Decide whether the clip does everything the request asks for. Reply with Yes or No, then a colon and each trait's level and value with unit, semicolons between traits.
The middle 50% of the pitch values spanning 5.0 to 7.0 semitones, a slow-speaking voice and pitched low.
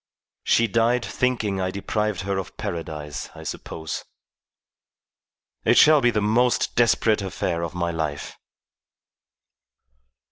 Yes: wide, 5.4 semitones; slow, 115 wpm; low, 100 Hz